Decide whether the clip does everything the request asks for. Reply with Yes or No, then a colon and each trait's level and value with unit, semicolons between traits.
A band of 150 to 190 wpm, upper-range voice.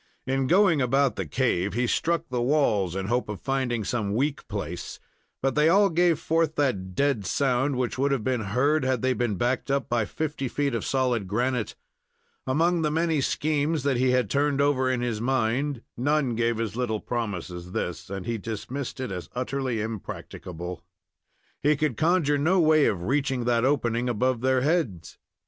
No: average, 185 wpm; low, 130 Hz